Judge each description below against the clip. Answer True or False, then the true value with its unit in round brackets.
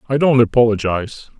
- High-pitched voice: False (115 Hz)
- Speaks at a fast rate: False (130 wpm)